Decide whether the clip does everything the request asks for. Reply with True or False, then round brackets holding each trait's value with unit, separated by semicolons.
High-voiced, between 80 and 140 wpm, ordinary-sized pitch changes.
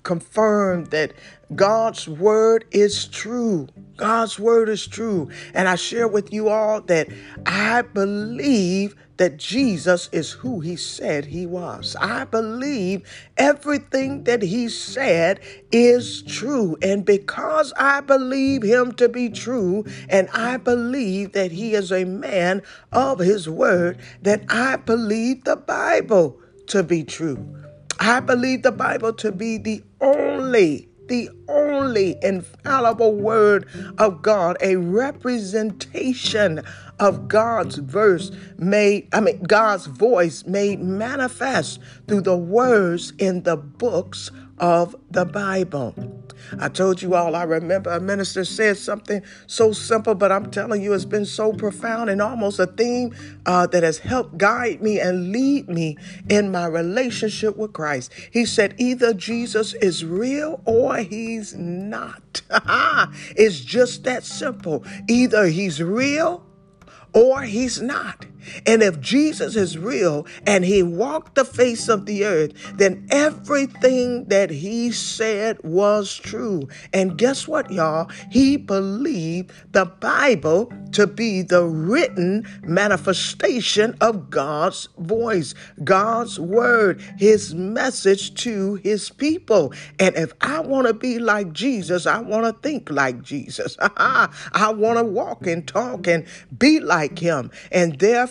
True (205 Hz; 135 wpm; 4.4 semitones)